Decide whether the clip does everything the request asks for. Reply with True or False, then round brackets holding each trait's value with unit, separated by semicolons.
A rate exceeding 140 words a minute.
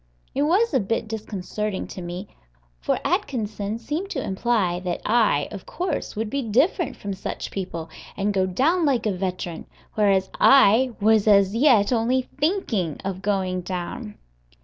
True (155 wpm)